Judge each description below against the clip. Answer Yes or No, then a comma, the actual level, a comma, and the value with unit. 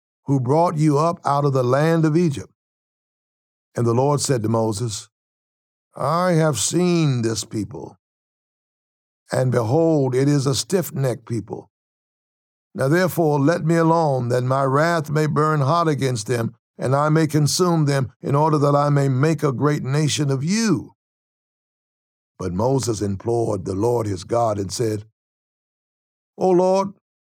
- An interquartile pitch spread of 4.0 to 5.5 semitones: Yes, average, 5.2 semitones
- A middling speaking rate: Yes, average, 150 wpm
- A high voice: No, medium, 140 Hz